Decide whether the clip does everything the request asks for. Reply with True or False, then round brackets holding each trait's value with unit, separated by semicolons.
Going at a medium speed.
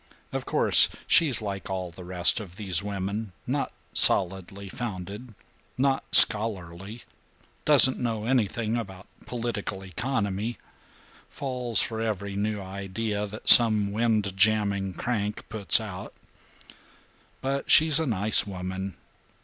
False (115 wpm)